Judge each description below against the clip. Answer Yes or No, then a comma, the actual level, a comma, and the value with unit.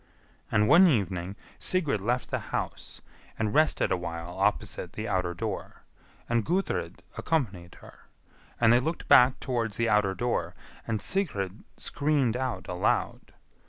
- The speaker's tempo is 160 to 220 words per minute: No, slow, 135 wpm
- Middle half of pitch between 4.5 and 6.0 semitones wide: Yes, wide, 5.5 semitones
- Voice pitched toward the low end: Yes, low, 115 Hz